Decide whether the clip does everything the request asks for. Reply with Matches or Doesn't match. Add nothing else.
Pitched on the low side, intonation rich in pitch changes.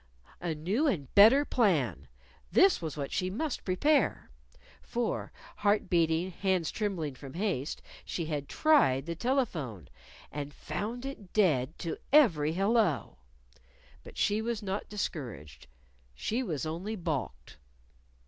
Doesn't match